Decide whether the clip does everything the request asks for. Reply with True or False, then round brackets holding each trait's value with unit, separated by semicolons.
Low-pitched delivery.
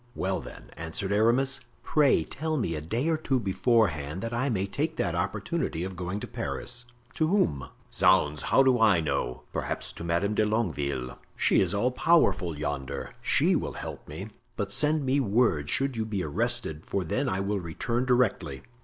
True (100 Hz)